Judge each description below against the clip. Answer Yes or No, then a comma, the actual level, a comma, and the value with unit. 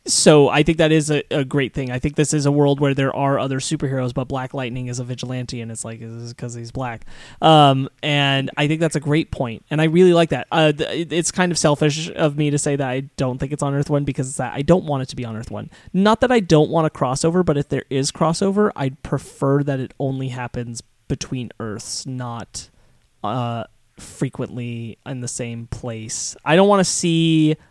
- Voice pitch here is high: No, medium, 140 Hz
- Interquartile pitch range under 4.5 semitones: Yes, average, 3.7 semitones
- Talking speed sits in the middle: No, fast, 235 wpm